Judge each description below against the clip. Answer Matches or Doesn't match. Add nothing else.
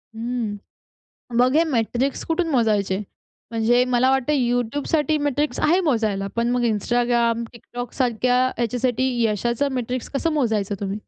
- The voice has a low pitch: Doesn't match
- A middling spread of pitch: Matches